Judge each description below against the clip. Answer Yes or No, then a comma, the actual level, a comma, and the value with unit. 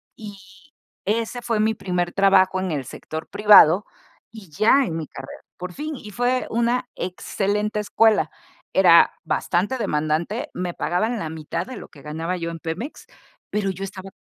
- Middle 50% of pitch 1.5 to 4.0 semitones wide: No, average, 4.6 semitones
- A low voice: No, high, 195 Hz